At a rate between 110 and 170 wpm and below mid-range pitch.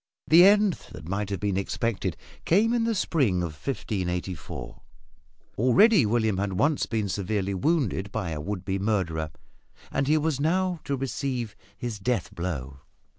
Yes: average, 155 wpm; low, 110 Hz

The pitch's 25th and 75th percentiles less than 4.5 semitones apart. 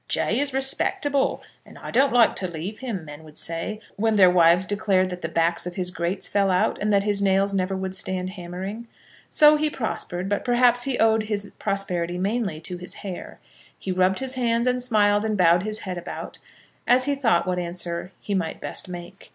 Yes: average, 3.9 semitones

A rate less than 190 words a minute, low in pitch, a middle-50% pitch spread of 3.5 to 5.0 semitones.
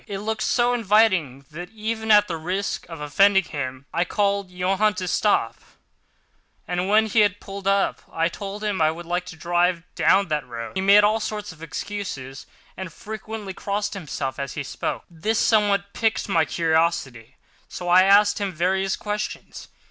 No: average, 170 wpm; high, 190 Hz; average, 4.1 semitones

